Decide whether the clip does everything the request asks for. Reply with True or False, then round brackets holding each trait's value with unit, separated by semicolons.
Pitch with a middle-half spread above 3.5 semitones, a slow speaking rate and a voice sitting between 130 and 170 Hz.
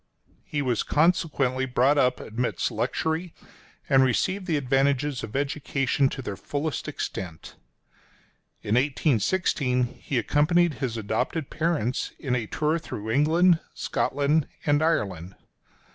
True (3.9 semitones; 120 wpm; 140 Hz)